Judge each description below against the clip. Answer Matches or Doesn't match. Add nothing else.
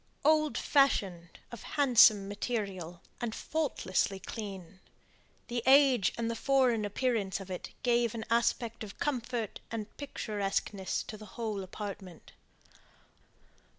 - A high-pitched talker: Matches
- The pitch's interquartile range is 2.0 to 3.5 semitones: Doesn't match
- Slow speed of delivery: Matches